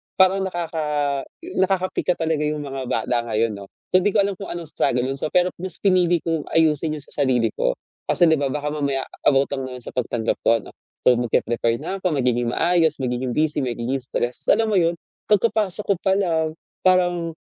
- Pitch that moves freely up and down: Yes, wide, 6.0 semitones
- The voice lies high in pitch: No, medium, 155 Hz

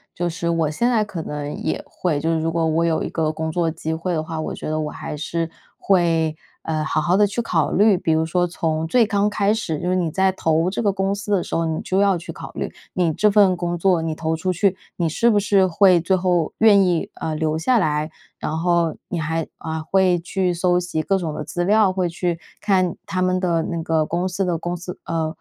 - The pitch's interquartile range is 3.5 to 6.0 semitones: No, average, 2.8 semitones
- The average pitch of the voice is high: No, medium, 175 Hz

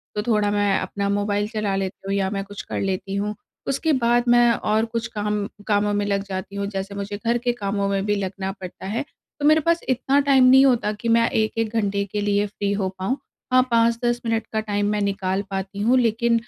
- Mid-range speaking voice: No, high, 205 Hz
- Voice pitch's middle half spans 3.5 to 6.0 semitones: No, narrow, 2.6 semitones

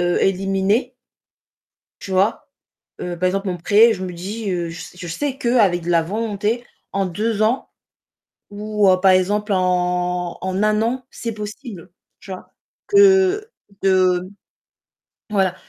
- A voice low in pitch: No, high, 195 Hz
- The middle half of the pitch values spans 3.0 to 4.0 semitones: Yes, average, 3.5 semitones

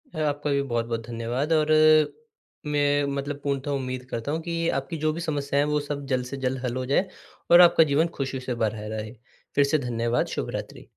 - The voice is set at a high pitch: No, medium, 140 Hz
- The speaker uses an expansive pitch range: No, average, 2.9 semitones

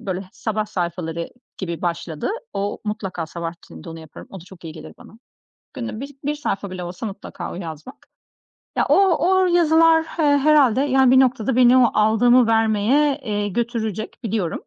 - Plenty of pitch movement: Yes, wide, 6.5 semitones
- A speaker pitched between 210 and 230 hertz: Yes, high, 220 Hz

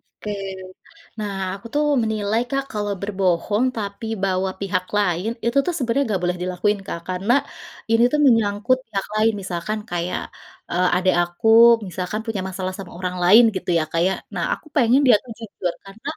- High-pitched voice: Yes, high, 200 Hz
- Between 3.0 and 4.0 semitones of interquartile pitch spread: Yes, average, 3.5 semitones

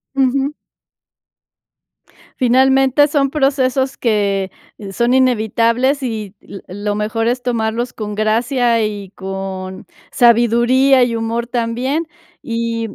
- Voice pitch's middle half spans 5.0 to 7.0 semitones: No, average, 3.2 semitones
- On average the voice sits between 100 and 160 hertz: No, high, 235 Hz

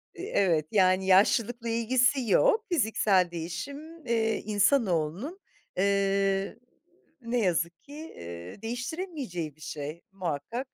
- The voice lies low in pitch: No, high, 200 Hz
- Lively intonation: Yes, wide, 6.3 semitones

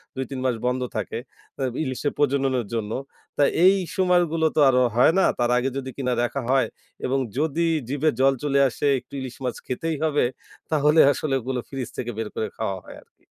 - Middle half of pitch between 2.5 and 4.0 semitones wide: Yes, average, 3.0 semitones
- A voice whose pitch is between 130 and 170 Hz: Yes, low, 135 Hz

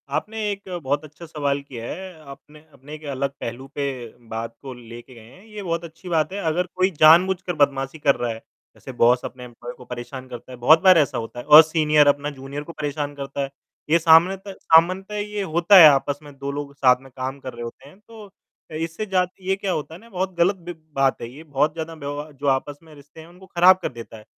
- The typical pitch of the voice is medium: Yes, medium, 150 Hz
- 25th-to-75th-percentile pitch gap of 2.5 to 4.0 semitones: No, average, 4.4 semitones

